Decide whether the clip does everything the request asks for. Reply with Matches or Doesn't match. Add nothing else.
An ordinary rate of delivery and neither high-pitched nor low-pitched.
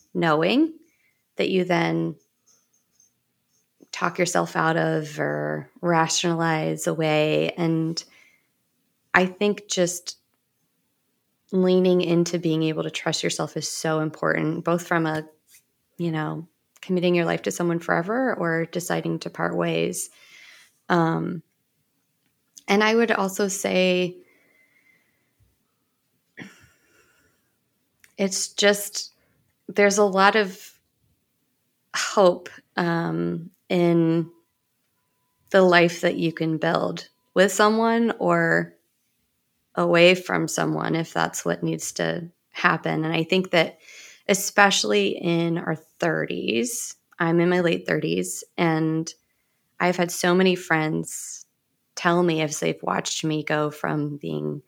Doesn't match